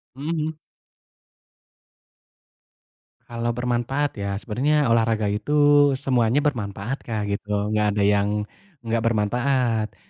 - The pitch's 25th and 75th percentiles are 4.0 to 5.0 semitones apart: Yes, average, 4.6 semitones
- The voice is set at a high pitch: No, low, 115 Hz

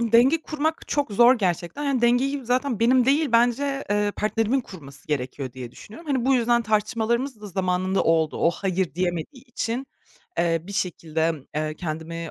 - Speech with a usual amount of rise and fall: No, wide, 6.9 semitones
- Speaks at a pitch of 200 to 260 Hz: Yes, high, 215 Hz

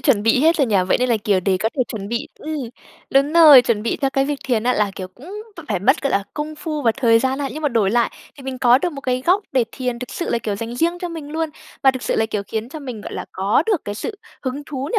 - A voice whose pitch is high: Yes, very high, 255 Hz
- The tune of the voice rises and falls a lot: No, average, 4.8 semitones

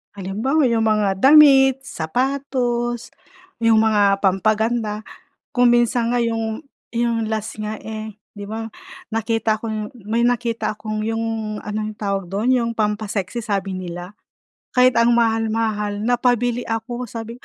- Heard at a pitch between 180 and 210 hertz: No, high, 225 Hz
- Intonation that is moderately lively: No, narrow, 2.1 semitones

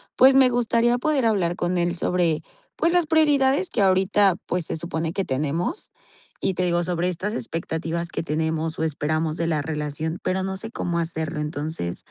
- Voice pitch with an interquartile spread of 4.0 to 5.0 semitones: Yes, average, 4.7 semitones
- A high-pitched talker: No, medium, 175 Hz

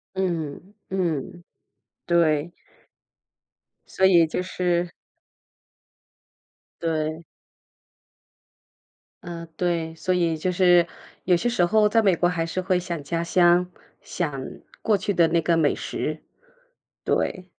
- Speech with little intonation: Yes, narrow, 1.9 semitones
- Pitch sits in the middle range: Yes, medium, 175 Hz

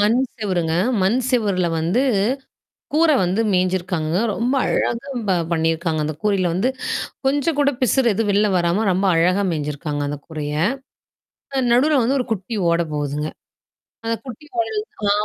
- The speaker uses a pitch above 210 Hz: No, high, 190 Hz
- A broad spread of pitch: Yes, wide, 6.4 semitones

